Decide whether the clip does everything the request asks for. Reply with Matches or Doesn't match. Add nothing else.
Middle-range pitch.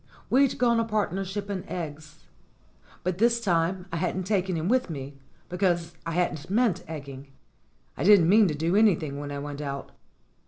Matches